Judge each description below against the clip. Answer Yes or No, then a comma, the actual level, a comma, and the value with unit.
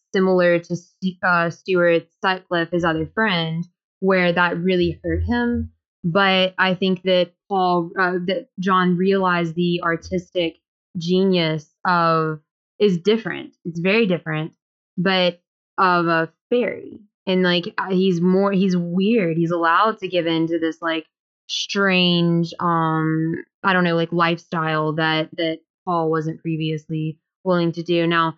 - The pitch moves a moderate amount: No, narrow, 2.1 semitones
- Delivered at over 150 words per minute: No, slow, 135 wpm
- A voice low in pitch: No, medium, 175 Hz